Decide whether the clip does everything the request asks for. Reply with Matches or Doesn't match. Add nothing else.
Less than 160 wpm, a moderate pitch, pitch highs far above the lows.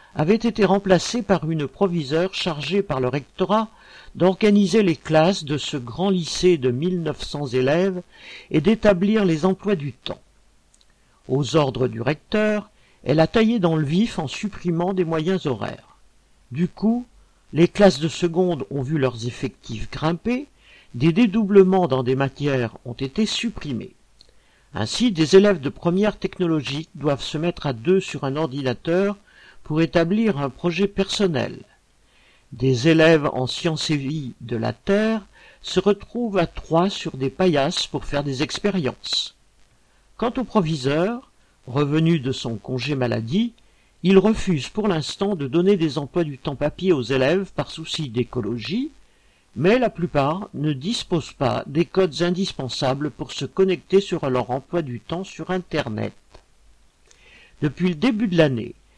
Matches